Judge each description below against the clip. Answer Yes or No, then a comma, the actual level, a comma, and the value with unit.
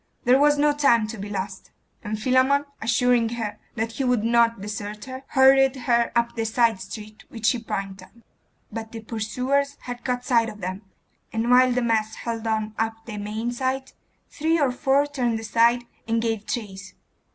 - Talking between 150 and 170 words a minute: No, average, 185 wpm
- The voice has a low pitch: No, high, 230 Hz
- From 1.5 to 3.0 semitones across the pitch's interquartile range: Yes, average, 2.7 semitones